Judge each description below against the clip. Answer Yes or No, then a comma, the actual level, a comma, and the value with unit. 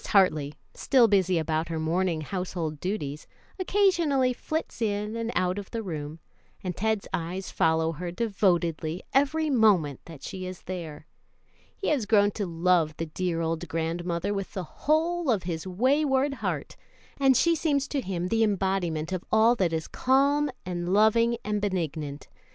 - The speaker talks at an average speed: Yes, average, 160 wpm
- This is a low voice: No, medium, 185 Hz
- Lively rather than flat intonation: Yes, wide, 5.8 semitones